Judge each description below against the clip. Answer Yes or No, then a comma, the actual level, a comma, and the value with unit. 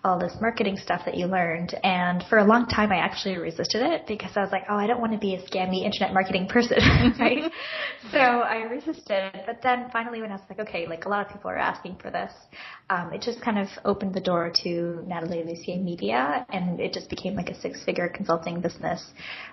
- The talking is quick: Yes, fast, 225 wpm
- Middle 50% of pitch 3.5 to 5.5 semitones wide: Yes, average, 4.1 semitones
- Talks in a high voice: Yes, high, 195 Hz